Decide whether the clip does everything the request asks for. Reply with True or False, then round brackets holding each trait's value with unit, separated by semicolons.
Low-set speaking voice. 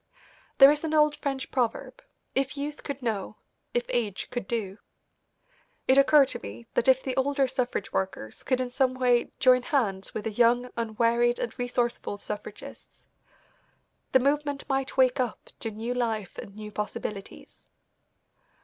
False (245 Hz)